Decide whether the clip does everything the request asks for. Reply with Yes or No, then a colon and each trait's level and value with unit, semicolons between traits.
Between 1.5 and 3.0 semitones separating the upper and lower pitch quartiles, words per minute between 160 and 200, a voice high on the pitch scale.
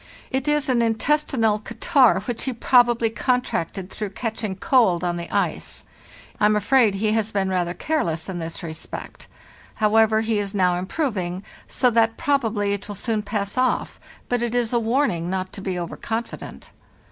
No: average, 4.2 semitones; average, 170 wpm; high, 220 Hz